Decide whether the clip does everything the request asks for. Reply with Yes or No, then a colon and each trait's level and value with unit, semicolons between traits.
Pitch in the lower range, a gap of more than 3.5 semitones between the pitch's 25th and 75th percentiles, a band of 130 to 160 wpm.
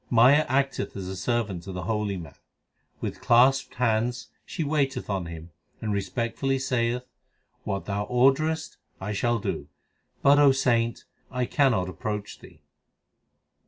Yes: low, 120 Hz; average, 5.0 semitones; average, 140 wpm